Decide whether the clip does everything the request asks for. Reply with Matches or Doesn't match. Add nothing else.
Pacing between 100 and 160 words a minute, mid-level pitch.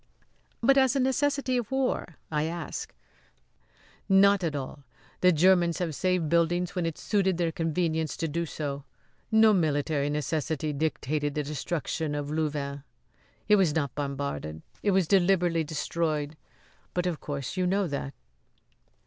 Matches